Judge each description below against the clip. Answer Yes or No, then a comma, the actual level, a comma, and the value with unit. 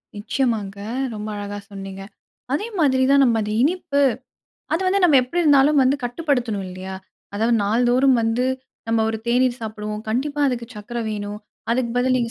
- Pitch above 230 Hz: Yes, high, 240 Hz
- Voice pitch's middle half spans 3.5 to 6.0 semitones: Yes, average, 4.2 semitones